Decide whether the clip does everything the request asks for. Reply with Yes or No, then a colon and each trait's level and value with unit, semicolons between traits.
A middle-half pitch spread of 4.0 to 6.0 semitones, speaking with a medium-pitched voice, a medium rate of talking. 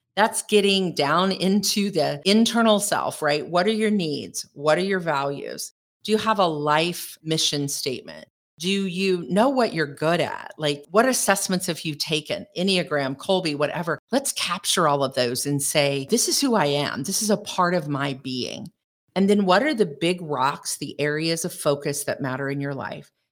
Yes: average, 5.2 semitones; medium, 175 Hz; average, 190 wpm